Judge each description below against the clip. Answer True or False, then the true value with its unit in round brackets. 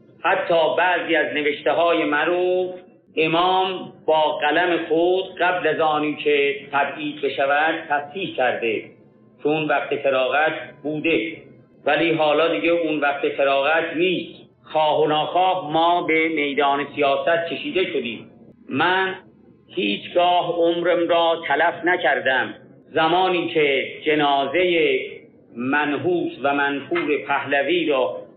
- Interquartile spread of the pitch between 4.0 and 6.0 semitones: False (3.3 semitones)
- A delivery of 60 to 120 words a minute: True (110 wpm)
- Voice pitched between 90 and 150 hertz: False (165 Hz)